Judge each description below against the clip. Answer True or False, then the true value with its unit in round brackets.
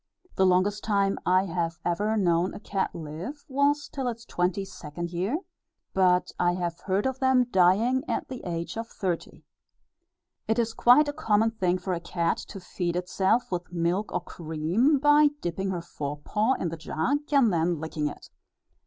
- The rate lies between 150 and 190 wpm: True (175 wpm)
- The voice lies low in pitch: False (185 Hz)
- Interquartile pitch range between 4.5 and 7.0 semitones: True (4.9 semitones)